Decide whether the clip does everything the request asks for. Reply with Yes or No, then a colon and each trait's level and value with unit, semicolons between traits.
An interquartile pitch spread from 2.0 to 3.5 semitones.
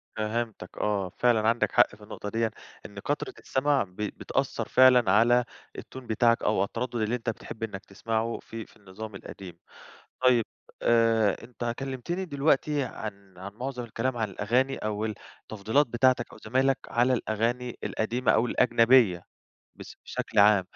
Yes: average, 2.9 semitones